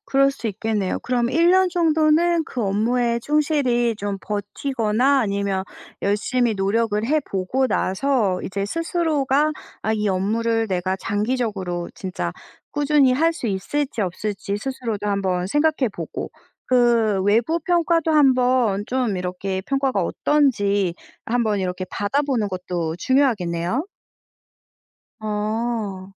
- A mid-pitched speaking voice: No, high, 225 Hz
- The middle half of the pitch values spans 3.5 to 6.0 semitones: Yes, wide, 5.6 semitones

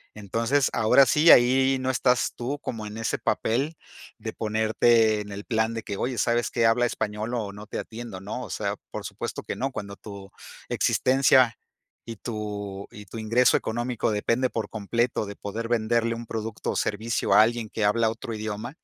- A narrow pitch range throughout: Yes, narrow, 2.1 semitones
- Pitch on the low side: Yes, low, 115 Hz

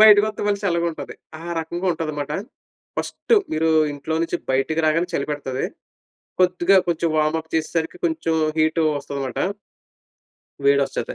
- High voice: No, medium, 160 Hz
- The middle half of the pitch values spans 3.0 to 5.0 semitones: No, narrow, 2.4 semitones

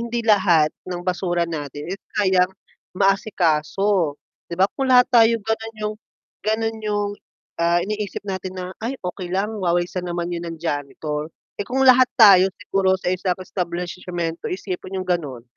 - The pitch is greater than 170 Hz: Yes, medium, 185 Hz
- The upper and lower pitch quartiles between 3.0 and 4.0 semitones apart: Yes, average, 3.4 semitones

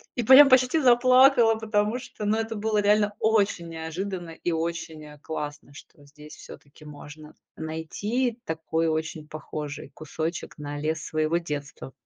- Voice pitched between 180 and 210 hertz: No, medium, 165 Hz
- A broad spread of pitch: Yes, wide, 6.1 semitones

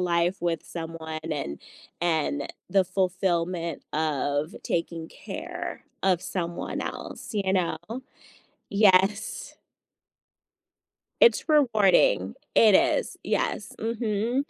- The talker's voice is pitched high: No, medium, 180 Hz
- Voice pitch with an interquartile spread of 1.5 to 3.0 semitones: No, average, 3.7 semitones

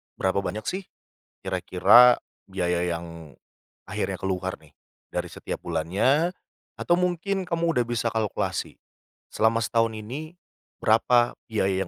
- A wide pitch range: Yes, wide, 6.3 semitones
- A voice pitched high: No, low, 110 Hz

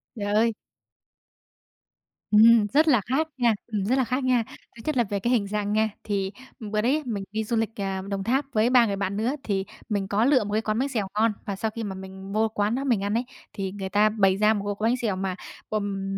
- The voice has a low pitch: No, high, 215 Hz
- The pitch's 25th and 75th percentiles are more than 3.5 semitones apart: No, average, 2.8 semitones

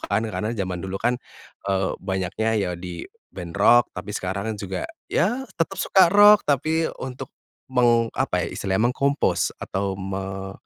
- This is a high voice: No, low, 105 Hz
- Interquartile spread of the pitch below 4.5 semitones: No, wide, 5.4 semitones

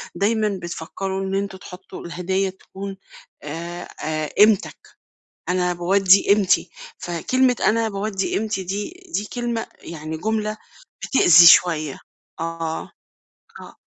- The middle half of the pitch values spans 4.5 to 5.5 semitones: No, average, 3.3 semitones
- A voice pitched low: No, high, 190 Hz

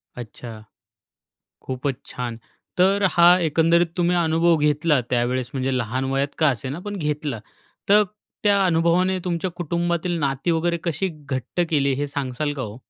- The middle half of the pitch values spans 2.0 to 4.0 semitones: No, average, 4.7 semitones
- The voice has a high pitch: No, medium, 155 Hz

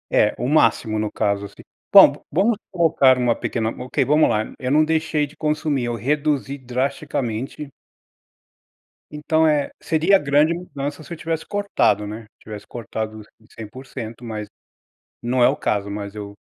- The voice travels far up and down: Yes, wide, 5.7 semitones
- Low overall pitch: Yes, low, 130 Hz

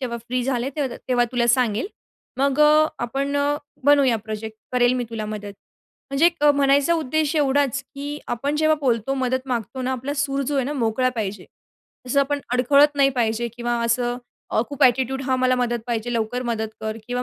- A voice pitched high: Yes, very high, 255 Hz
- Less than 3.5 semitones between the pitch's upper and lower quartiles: Yes, average, 3.0 semitones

